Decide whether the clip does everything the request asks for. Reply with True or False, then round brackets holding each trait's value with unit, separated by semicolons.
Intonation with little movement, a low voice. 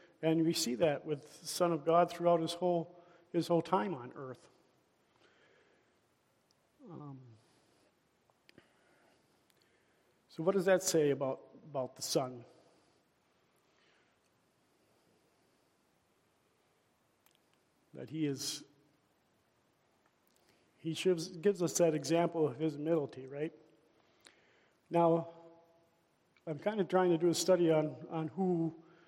False (2.0 semitones; 165 Hz)